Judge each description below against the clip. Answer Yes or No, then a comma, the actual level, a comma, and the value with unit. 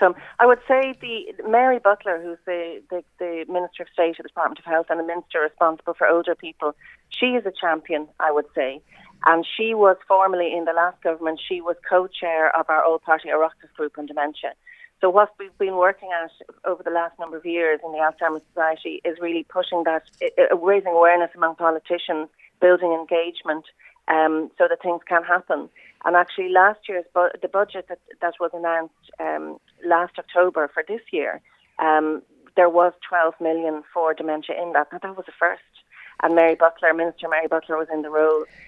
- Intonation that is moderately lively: No, narrow, 2.1 semitones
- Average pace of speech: Yes, average, 190 wpm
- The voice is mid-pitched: Yes, medium, 170 Hz